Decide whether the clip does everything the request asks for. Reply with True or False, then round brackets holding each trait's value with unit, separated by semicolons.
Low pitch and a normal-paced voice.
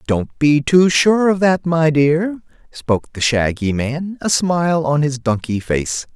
False (150 Hz; 175 wpm)